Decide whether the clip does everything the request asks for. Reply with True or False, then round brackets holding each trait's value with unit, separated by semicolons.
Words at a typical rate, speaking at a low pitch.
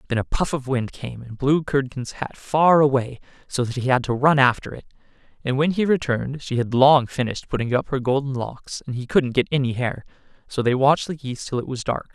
False (235 wpm; 130 Hz)